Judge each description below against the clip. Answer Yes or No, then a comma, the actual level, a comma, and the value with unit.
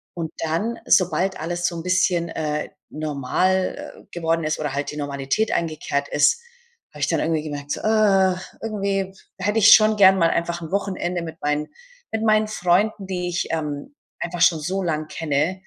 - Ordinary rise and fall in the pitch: Yes, average, 3.8 semitones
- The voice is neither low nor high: Yes, medium, 175 Hz